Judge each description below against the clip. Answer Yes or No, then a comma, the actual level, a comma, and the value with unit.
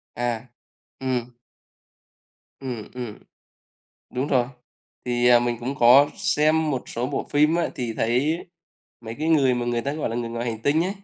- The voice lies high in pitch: No, low, 125 Hz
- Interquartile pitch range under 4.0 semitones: Yes, average, 3.4 semitones